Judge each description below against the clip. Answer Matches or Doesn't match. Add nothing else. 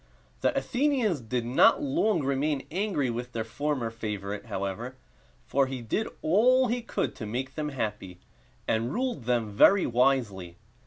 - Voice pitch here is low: Matches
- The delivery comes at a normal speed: Matches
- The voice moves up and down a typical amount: Doesn't match